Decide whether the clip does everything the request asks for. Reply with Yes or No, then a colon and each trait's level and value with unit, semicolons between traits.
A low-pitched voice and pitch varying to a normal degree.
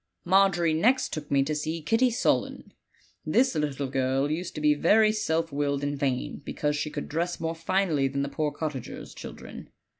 No: medium, 155 Hz; average, 3.6 semitones